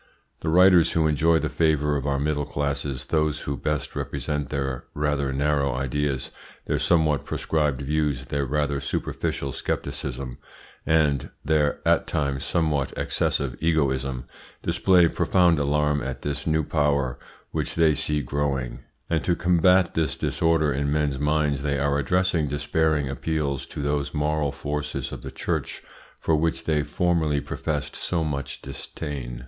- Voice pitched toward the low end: Yes, very low, 75 Hz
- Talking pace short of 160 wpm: Yes, average, 145 wpm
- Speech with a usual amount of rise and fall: No, narrow, 2.0 semitones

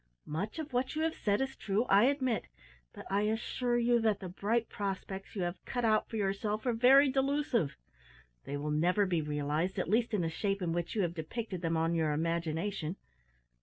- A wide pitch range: Yes, wide, 5.8 semitones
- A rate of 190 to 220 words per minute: Yes, fast, 205 wpm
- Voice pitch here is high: Yes, high, 200 Hz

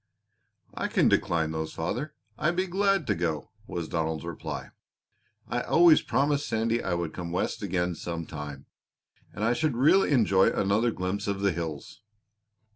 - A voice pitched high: No, low, 100 Hz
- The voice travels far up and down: Yes, wide, 8.5 semitones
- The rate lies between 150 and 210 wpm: Yes, average, 160 wpm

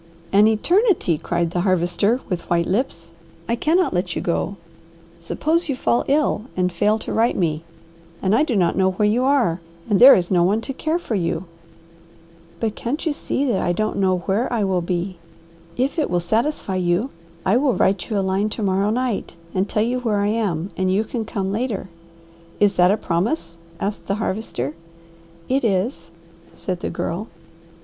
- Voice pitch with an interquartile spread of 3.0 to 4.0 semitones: No, average, 4.7 semitones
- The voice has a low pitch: No, high, 205 Hz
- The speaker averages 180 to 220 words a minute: Yes, average, 190 wpm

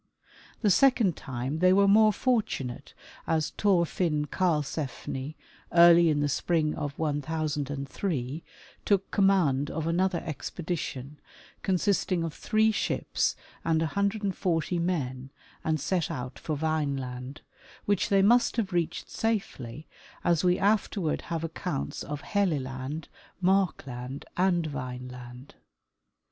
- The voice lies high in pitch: No, medium, 160 Hz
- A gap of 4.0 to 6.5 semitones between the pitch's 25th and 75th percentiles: Yes, average, 5.0 semitones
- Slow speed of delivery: Yes, slow, 115 wpm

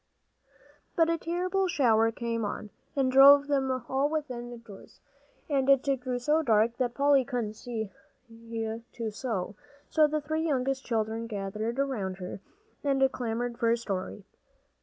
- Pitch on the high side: Yes, high, 245 Hz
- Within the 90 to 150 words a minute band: Yes, average, 145 wpm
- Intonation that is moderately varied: Yes, average, 3.8 semitones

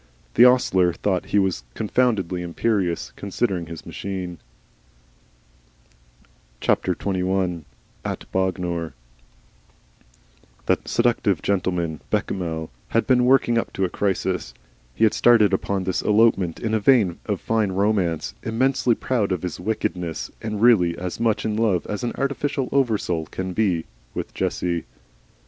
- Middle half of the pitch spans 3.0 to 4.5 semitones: Yes, average, 4.1 semitones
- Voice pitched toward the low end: Yes, very low, 95 Hz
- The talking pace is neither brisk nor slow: No, slow, 130 wpm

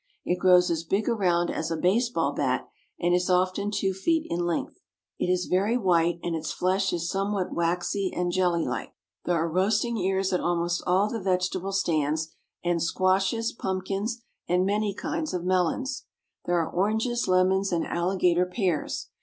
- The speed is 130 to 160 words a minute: No, average, 170 wpm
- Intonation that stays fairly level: Yes, narrow, 2.3 semitones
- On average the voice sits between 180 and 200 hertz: Yes, medium, 185 Hz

